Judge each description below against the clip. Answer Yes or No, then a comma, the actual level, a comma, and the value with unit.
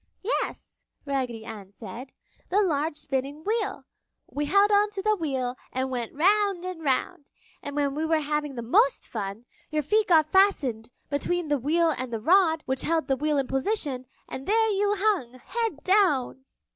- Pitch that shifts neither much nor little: No, wide, 6.6 semitones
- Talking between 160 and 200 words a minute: Yes, average, 175 wpm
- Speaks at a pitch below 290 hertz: No, very high, 295 Hz